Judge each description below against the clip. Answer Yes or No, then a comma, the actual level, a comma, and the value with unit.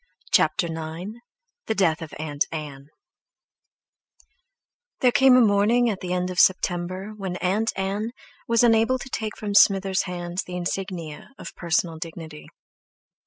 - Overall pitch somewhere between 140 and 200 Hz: Yes, medium, 185 Hz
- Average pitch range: Yes, average, 4.1 semitones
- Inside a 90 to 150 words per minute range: Yes, slow, 135 wpm